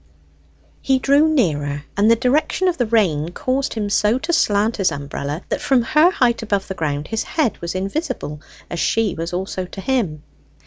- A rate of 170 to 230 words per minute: Yes, average, 185 wpm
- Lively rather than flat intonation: Yes, wide, 7.4 semitones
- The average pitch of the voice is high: Yes, high, 215 Hz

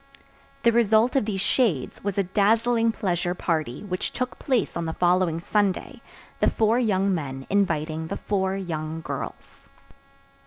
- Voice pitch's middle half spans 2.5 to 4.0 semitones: No, average, 4.8 semitones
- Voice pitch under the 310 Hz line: Yes, high, 190 Hz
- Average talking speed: Yes, average, 150 wpm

